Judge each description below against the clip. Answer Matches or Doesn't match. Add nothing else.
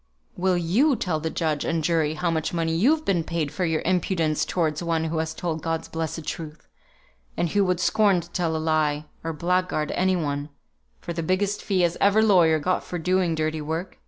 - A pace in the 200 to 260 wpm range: Matches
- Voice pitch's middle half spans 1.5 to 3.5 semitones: Matches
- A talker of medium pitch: Matches